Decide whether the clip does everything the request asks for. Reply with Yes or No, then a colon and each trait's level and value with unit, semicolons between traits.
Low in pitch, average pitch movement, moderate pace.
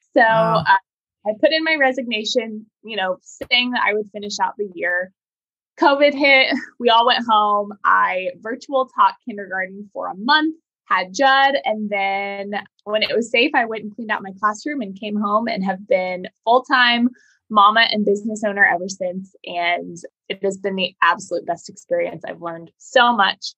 No: high, 215 Hz; average, 4.8 semitones; average, 180 wpm